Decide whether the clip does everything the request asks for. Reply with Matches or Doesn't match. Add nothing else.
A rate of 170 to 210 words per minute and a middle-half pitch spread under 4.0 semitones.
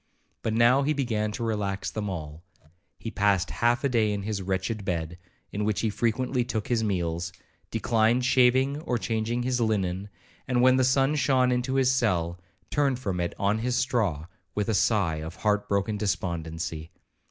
Doesn't match